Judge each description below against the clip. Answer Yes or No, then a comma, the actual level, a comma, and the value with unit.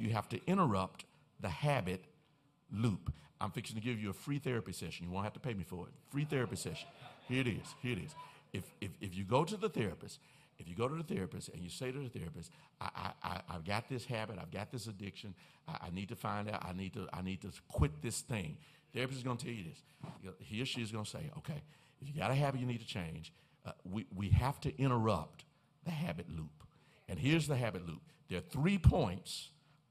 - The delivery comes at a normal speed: No, fast, 245 wpm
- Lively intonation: Yes, wide, 7.0 semitones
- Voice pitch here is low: Yes, low, 120 Hz